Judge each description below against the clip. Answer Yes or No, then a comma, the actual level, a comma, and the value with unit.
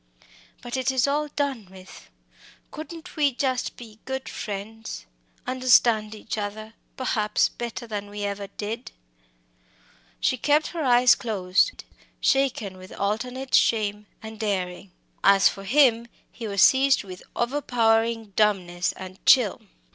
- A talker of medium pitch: No, high, 225 Hz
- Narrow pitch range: No, average, 4.1 semitones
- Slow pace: Yes, slow, 130 wpm